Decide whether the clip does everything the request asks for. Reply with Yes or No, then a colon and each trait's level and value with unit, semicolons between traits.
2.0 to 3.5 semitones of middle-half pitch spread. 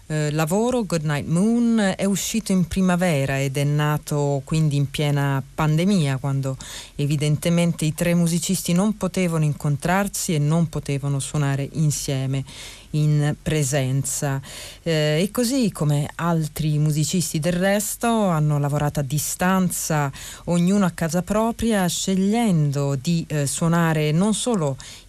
No: average, 4.1 semitones